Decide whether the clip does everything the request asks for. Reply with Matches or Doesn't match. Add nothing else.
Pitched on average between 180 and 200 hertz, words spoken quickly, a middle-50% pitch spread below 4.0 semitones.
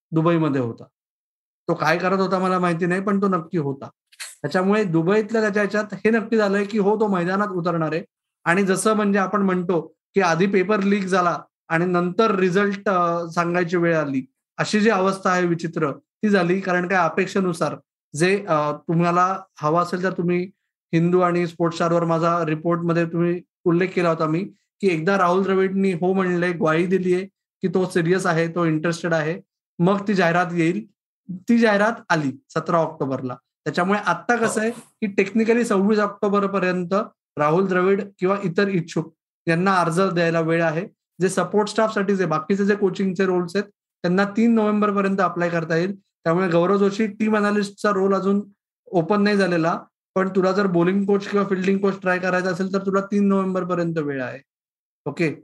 Matches